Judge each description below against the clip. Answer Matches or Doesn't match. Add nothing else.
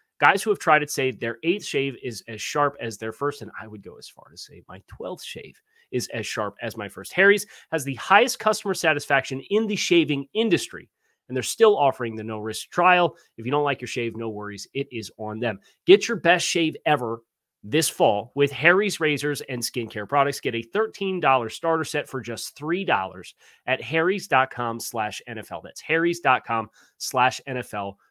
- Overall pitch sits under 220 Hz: Matches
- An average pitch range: Doesn't match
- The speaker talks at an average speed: Matches